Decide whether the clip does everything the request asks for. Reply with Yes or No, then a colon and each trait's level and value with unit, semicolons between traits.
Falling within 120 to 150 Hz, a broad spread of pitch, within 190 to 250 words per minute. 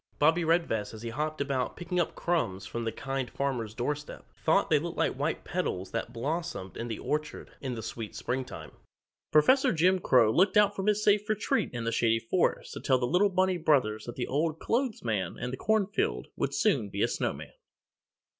Yes: medium, 140 Hz; wide, 7.3 semitones; average, 200 wpm